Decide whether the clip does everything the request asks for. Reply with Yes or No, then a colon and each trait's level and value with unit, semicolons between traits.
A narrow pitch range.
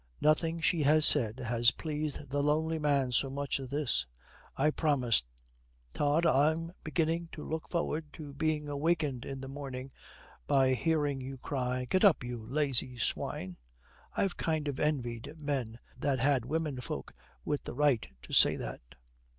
No: average, 3.2 semitones